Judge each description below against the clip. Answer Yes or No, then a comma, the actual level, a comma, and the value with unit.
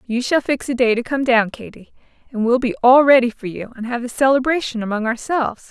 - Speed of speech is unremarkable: No, fast, 230 wpm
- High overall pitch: Yes, high, 245 Hz